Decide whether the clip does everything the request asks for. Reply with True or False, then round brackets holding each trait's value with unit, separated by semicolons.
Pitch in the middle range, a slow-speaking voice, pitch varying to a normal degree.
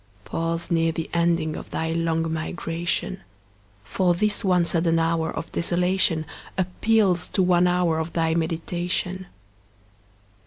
False (170 Hz; 125 wpm; 1.6 semitones)